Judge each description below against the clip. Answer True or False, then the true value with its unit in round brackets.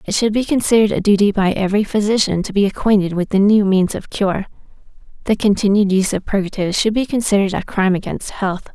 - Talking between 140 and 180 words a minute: False (205 wpm)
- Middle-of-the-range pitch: False (200 Hz)